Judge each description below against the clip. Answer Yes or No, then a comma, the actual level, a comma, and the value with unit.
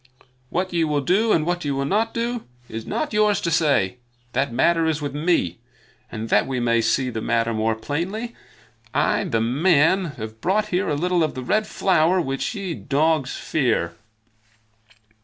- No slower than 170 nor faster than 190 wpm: Yes, average, 175 wpm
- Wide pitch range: Yes, wide, 7.1 semitones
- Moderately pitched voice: Yes, medium, 155 Hz